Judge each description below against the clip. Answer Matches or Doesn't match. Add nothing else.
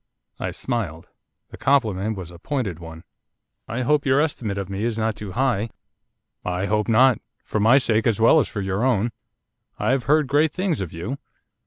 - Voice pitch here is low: Matches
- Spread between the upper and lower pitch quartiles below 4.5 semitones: Doesn't match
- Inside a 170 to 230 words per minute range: Matches